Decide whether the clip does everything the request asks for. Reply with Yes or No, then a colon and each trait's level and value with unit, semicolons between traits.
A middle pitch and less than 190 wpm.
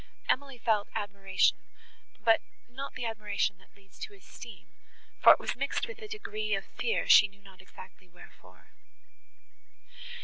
No: high, 225 Hz; average, 145 wpm